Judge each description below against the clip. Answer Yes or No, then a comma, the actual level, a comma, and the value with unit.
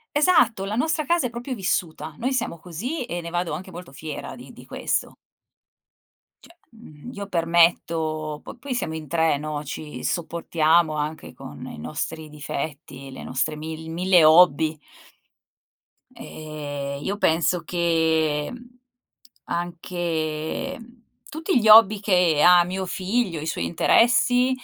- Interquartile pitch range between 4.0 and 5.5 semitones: Yes, average, 5.0 semitones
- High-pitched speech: No, medium, 170 Hz